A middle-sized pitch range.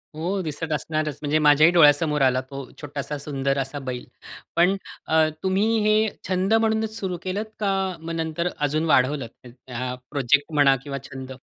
Yes: average, 4.0 semitones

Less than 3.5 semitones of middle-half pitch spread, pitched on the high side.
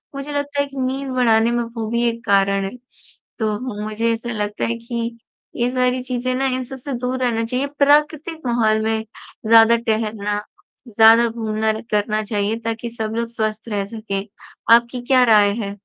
Yes: narrow, 2.6 semitones; high, 230 Hz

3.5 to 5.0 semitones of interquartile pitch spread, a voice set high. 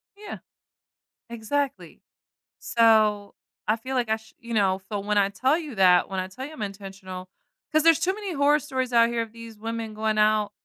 Yes: average, 4.1 semitones; high, 225 Hz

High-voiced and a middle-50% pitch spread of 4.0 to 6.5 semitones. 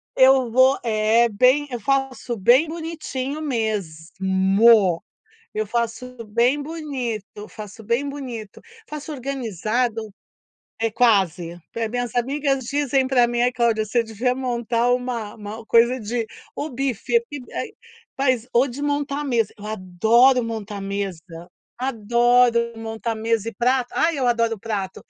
No: high, 235 Hz; average, 3.2 semitones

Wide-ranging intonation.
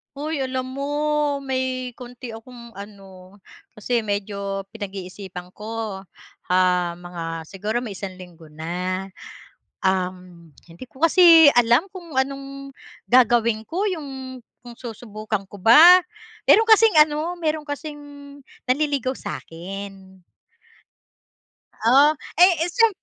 Yes: wide, 6.3 semitones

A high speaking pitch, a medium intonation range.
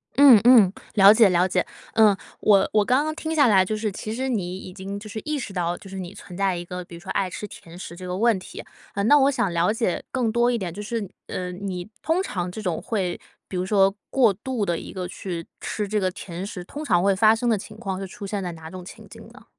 Yes: high, 195 Hz; average, 3.5 semitones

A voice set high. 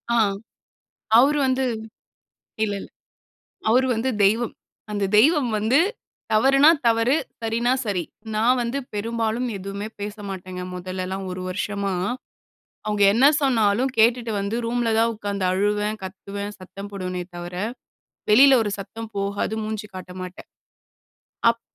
Yes: high, 215 Hz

